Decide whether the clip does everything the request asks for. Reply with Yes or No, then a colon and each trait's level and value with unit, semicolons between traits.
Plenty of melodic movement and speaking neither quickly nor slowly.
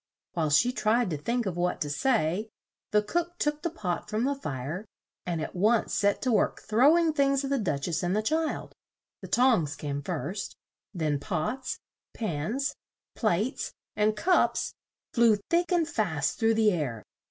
Yes: wide, 7.9 semitones; average, 175 wpm